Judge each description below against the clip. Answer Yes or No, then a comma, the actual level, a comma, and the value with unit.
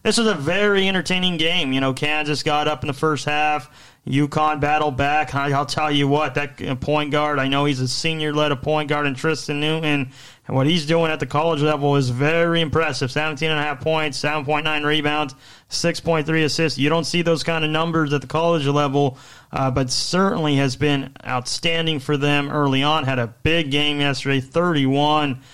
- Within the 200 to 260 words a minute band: Yes, fast, 205 wpm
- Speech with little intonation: Yes, narrow, 1.9 semitones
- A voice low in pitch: No, medium, 150 Hz